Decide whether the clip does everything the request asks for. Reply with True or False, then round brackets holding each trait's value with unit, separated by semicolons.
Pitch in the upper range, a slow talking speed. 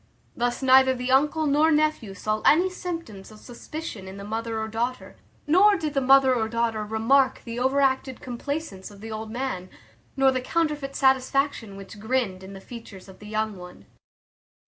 False (250 Hz; 175 wpm)